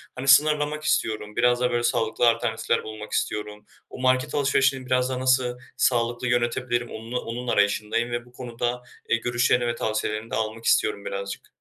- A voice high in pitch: No, low, 120 Hz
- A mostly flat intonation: Yes, narrow, 2.1 semitones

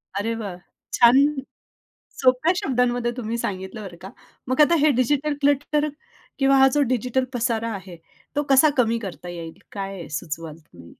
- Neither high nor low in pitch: No, high, 235 Hz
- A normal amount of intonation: No, wide, 5.9 semitones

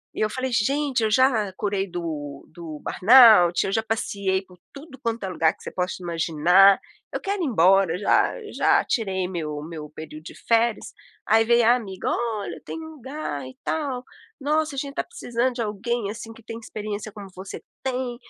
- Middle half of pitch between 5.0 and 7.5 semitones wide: Yes, average, 5.3 semitones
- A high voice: Yes, high, 215 Hz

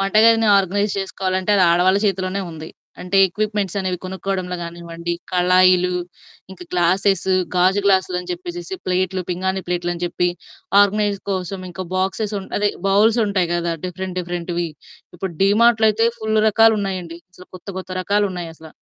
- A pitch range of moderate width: No, narrow, 2.2 semitones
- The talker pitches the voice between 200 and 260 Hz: No, medium, 185 Hz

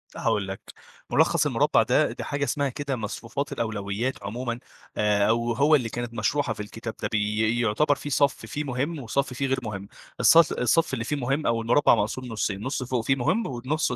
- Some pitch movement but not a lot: Yes, average, 4.1 semitones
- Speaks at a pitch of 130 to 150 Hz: No, low, 120 Hz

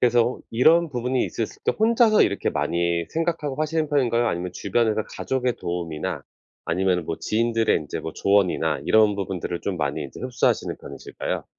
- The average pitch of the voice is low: Yes, low, 115 Hz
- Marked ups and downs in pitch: Yes, wide, 6.8 semitones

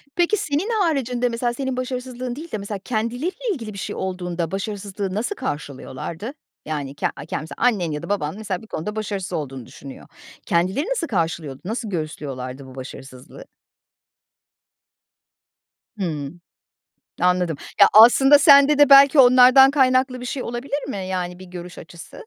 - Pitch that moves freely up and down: Yes, wide, 7.4 semitones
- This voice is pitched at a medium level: No, high, 210 Hz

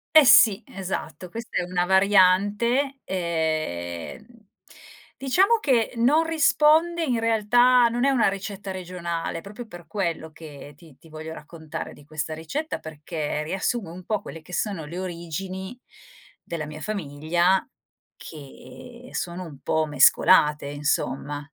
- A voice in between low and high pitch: Yes, medium, 180 Hz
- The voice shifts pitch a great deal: Yes, wide, 6.6 semitones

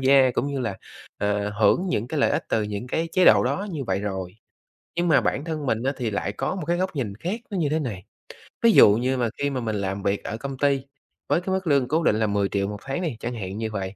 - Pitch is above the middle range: No, low, 125 Hz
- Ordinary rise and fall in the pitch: No, wide, 6.8 semitones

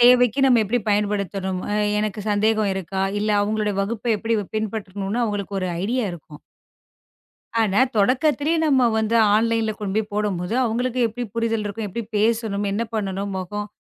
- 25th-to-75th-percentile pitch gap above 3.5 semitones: No, narrow, 2.5 semitones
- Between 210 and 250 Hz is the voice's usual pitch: Yes, high, 215 Hz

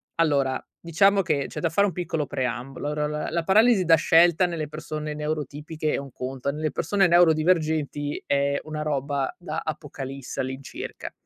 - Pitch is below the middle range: No, medium, 150 Hz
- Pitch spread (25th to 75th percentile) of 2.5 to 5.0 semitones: Yes, average, 2.9 semitones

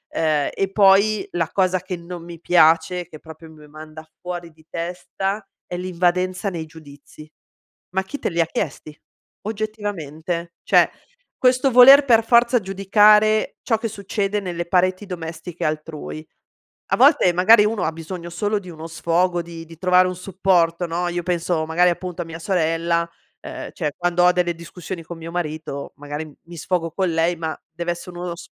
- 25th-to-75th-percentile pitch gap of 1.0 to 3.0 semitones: Yes, average, 2.7 semitones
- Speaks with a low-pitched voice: No, medium, 175 Hz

